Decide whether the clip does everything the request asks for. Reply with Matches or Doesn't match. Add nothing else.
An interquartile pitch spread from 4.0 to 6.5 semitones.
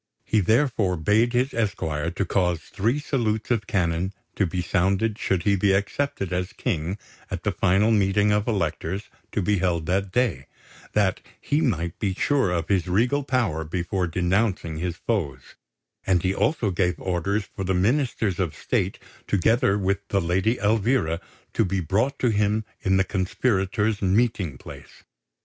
Doesn't match